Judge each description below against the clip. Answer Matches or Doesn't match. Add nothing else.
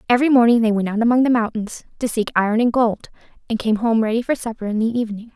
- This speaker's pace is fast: Matches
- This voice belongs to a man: Doesn't match